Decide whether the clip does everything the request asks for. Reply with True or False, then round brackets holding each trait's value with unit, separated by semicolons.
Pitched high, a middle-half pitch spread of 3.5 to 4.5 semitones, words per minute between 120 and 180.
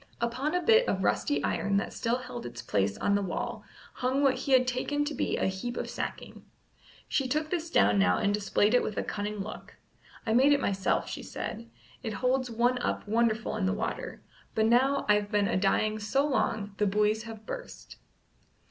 False (225 Hz; 4.1 semitones; 200 wpm)